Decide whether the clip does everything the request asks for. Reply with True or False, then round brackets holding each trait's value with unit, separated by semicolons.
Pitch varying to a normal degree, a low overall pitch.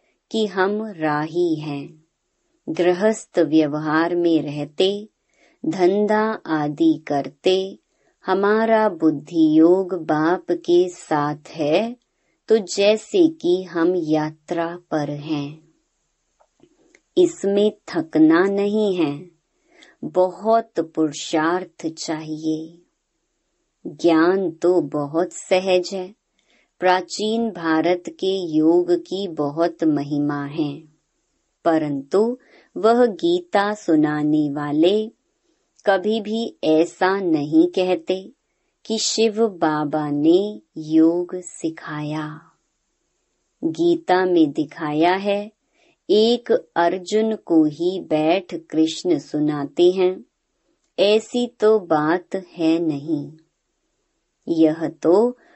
False (4.7 semitones; 175 Hz)